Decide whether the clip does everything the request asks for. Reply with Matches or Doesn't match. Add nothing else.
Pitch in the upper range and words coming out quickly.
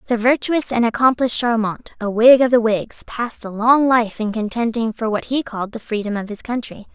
Matches